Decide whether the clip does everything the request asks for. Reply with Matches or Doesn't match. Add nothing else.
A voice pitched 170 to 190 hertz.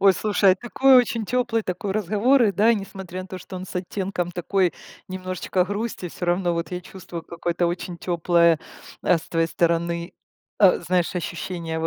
Matches